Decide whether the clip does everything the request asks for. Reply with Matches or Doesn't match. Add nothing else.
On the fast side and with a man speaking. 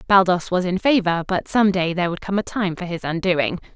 Doesn't match